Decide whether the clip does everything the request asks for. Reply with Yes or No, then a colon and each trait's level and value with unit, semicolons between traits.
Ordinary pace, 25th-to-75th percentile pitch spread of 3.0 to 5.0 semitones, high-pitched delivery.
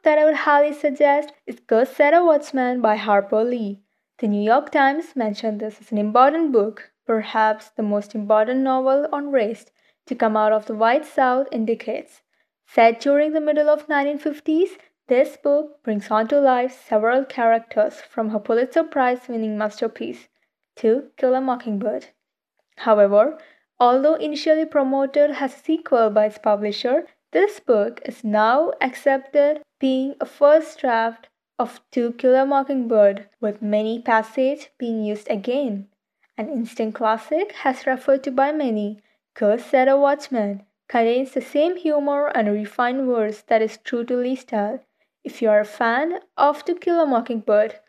Yes: average, 160 wpm; average, 4.7 semitones; very high, 255 Hz